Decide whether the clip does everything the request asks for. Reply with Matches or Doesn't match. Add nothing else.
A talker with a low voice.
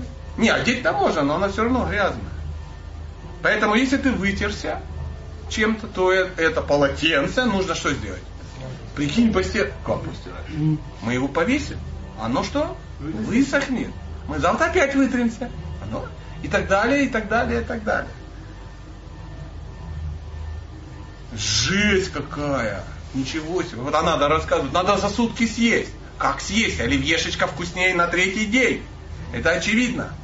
Doesn't match